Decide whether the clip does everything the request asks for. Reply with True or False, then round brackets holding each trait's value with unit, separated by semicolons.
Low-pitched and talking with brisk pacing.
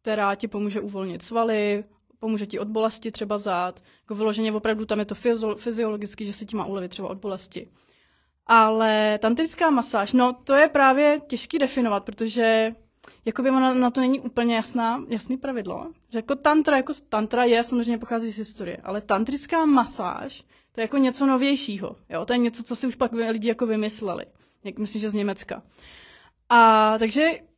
False (225 Hz; 180 wpm)